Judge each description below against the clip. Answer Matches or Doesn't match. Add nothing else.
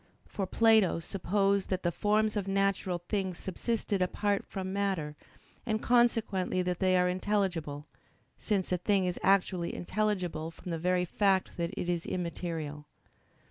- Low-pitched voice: Doesn't match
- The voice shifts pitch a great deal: Doesn't match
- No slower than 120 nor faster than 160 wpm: Matches